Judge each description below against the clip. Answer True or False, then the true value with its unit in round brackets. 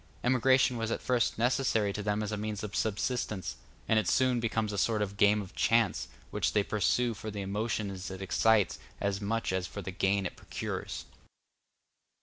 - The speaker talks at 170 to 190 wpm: True (185 wpm)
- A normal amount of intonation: False (2.3 semitones)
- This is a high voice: False (105 Hz)